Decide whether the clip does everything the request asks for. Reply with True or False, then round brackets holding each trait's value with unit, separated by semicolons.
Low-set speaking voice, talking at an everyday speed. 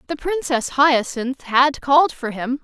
False (270 Hz; 160 wpm)